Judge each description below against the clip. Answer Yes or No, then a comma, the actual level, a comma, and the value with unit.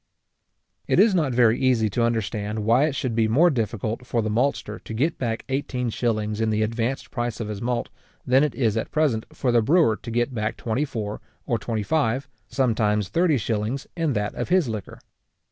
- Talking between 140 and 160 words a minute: No, average, 200 wpm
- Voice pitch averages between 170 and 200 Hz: No, low, 115 Hz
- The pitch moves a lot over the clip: No, average, 3.4 semitones